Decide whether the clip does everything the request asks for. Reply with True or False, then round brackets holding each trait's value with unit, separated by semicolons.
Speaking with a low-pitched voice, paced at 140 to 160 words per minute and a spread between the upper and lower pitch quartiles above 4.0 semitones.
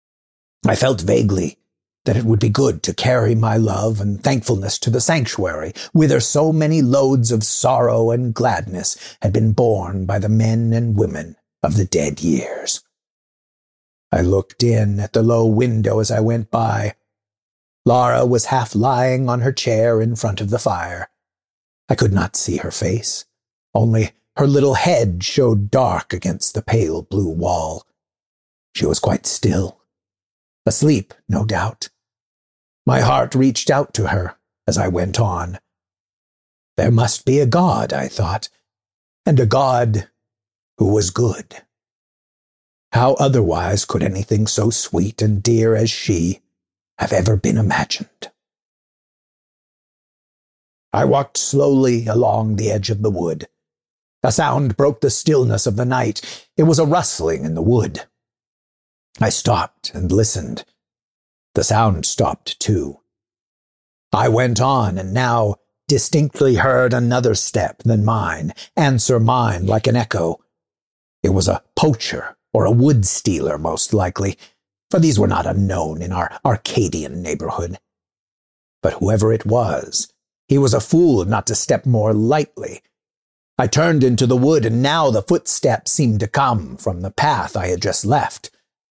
True (110 Hz; 150 wpm; 4.5 semitones)